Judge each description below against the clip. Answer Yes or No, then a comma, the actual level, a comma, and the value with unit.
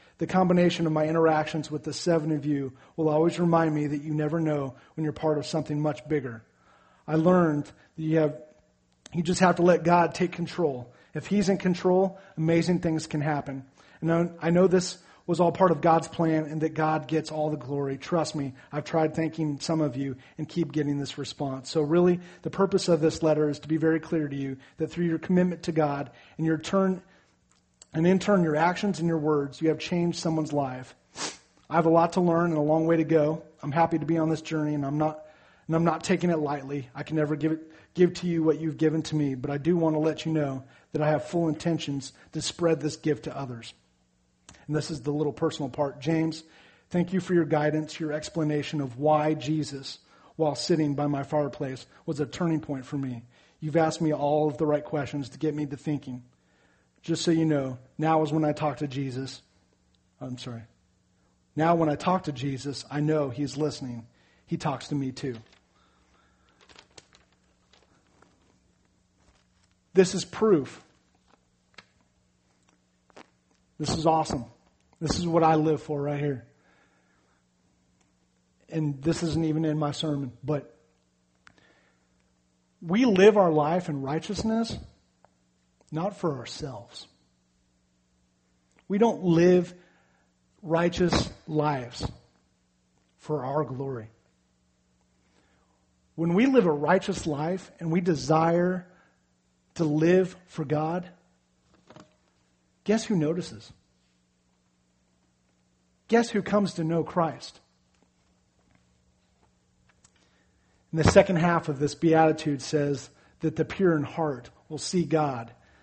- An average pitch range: Yes, average, 4.1 semitones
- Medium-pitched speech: Yes, medium, 150 Hz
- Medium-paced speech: Yes, average, 165 wpm